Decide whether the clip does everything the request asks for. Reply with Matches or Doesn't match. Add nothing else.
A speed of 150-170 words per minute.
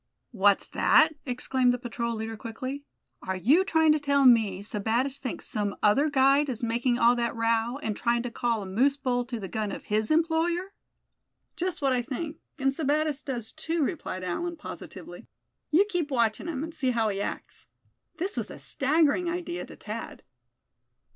Doesn't match